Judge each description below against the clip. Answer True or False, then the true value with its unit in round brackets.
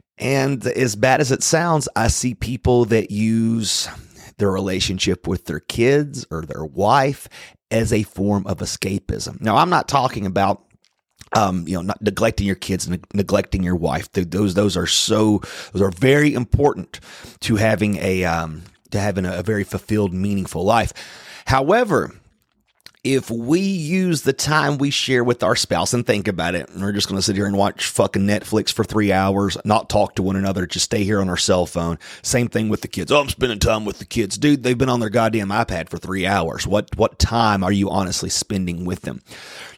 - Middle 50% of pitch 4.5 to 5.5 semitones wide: False (4.0 semitones)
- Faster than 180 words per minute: True (200 wpm)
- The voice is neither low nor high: False (105 Hz)